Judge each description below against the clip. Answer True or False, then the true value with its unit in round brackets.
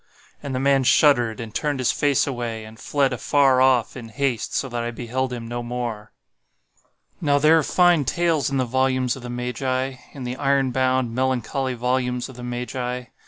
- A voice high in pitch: False (130 Hz)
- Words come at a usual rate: True (185 wpm)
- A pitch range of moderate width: False (2.0 semitones)